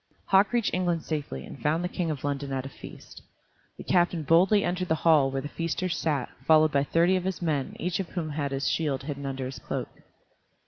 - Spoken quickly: Yes, fast, 225 wpm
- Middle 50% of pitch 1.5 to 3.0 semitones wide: No, average, 3.9 semitones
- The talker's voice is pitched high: No, medium, 160 Hz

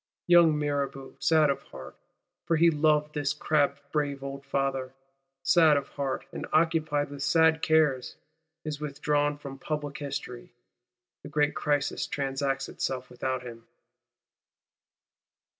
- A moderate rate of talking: No, slow, 125 wpm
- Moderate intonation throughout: No, narrow, 2.0 semitones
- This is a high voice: No, medium, 145 Hz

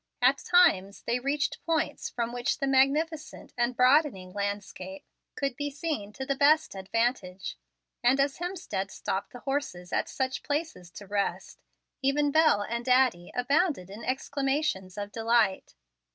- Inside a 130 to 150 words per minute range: Yes, average, 145 wpm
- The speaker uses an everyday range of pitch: No, wide, 6.1 semitones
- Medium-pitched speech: No, very high, 250 Hz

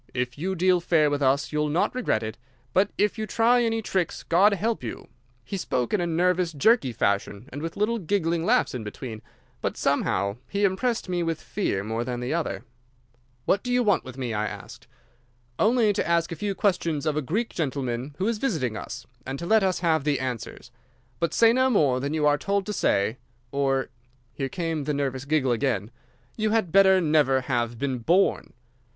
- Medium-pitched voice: Yes, medium, 155 Hz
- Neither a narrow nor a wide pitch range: No, wide, 7.1 semitones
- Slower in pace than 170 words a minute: No, average, 195 wpm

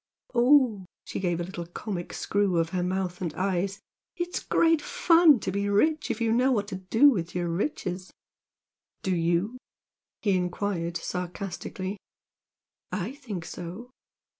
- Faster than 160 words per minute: No, average, 155 wpm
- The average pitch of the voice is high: Yes, high, 195 Hz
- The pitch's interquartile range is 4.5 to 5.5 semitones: Yes, average, 5.0 semitones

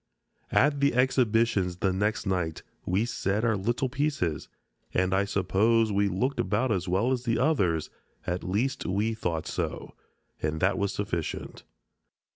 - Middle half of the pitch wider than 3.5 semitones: Yes, average, 4.4 semitones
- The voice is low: Yes, low, 100 Hz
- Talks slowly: No, average, 150 wpm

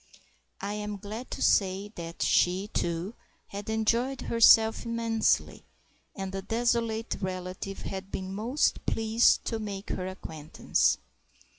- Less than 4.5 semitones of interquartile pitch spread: Yes, average, 3.1 semitones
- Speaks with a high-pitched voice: Yes, high, 205 Hz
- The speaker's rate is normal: No, slow, 125 wpm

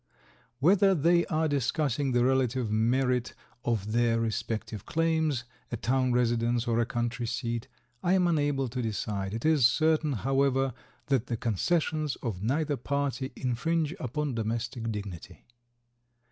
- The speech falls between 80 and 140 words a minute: Yes, slow, 135 wpm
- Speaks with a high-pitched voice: No, low, 125 Hz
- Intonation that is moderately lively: Yes, average, 4.1 semitones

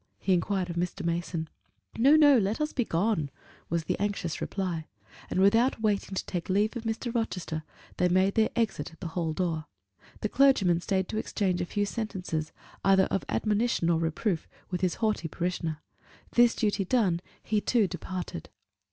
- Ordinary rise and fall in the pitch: Yes, average, 4.2 semitones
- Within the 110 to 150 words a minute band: No, average, 175 wpm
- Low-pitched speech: No, high, 190 Hz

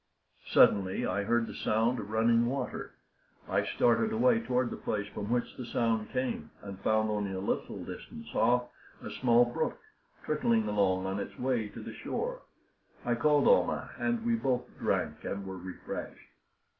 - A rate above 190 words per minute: No, average, 170 wpm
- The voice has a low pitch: Yes, low, 115 Hz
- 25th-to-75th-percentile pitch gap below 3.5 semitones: No, average, 3.9 semitones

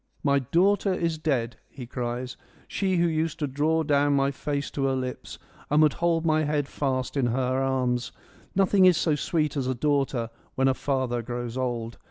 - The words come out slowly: No, fast, 205 wpm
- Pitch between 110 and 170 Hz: Yes, medium, 140 Hz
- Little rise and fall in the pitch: No, average, 3.6 semitones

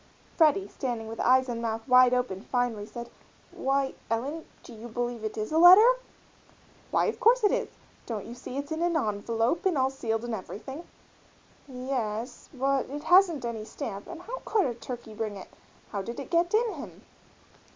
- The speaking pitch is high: Yes, very high, 250 Hz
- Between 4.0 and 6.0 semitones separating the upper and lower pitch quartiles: Yes, wide, 5.6 semitones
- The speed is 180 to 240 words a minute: Yes, average, 185 wpm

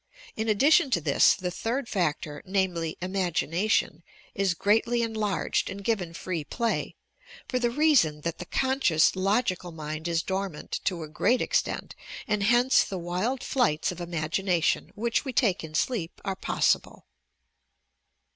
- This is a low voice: No, high, 190 Hz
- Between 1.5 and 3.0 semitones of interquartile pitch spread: No, wide, 5.5 semitones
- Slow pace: No, average, 145 wpm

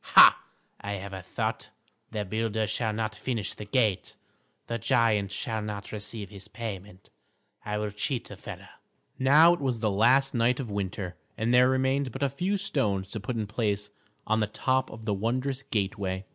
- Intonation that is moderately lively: Yes, average, 3.8 semitones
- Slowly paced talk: No, average, 185 wpm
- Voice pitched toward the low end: Yes, low, 110 Hz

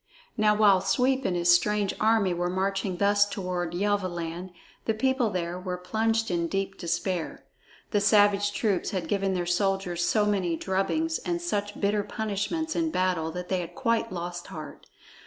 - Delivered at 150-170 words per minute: Yes, average, 165 wpm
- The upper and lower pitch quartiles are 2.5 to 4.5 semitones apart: Yes, average, 3.0 semitones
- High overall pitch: Yes, high, 195 Hz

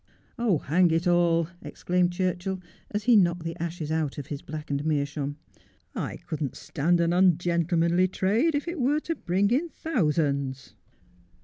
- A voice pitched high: No, medium, 175 Hz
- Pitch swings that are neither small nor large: Yes, average, 3.5 semitones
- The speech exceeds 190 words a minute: No, average, 170 wpm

